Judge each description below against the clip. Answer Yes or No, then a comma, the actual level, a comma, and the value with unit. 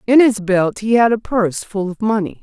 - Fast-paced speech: Yes, fast, 250 wpm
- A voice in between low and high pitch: No, high, 210 Hz